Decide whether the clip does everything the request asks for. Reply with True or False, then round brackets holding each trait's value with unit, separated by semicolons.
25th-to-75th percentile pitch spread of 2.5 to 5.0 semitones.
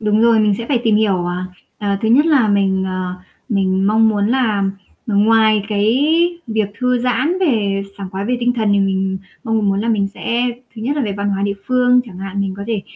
True (2.8 semitones)